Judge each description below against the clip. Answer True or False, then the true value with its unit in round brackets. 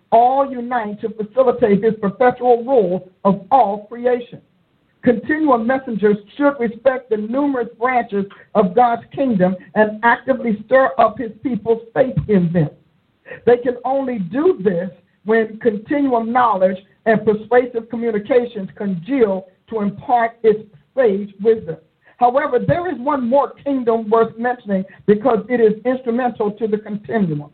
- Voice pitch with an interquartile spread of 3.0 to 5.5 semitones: True (3.4 semitones)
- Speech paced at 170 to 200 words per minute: False (135 wpm)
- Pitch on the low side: False (230 Hz)